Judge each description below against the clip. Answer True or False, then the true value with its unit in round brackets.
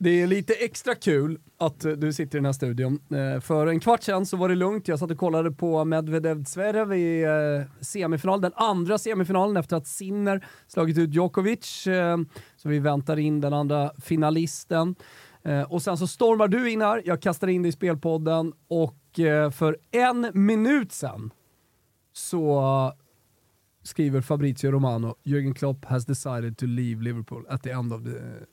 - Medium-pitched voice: True (160 Hz)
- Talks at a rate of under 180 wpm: True (165 wpm)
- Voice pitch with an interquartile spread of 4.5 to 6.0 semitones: True (5.0 semitones)